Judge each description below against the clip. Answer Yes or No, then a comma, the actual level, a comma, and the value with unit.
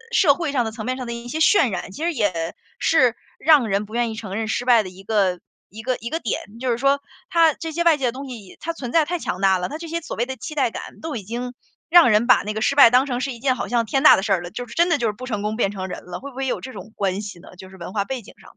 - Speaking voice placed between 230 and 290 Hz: Yes, high, 240 Hz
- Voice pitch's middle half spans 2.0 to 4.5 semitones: No, average, 5.1 semitones